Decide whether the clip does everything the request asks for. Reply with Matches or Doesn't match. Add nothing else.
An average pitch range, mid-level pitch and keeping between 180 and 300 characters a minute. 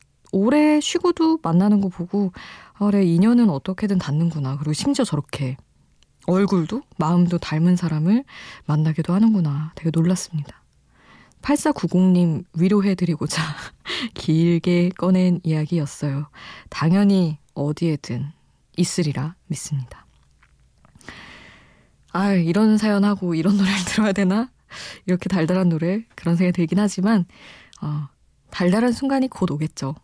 Matches